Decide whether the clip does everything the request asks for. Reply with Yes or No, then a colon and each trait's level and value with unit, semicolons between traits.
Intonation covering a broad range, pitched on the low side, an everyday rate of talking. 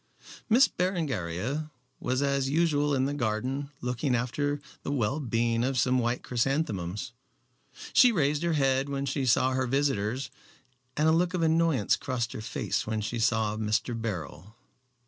No: average, 4.0 semitones; low, 130 Hz; average, 155 wpm